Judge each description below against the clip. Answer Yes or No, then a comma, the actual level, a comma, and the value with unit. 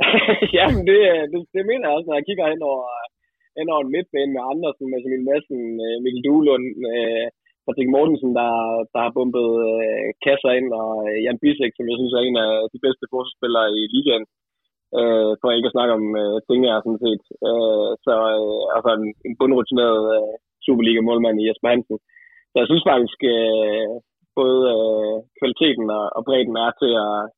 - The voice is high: No, low, 120 Hz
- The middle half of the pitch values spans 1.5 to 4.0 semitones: Yes, average, 3.6 semitones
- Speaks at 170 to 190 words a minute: Yes, average, 185 wpm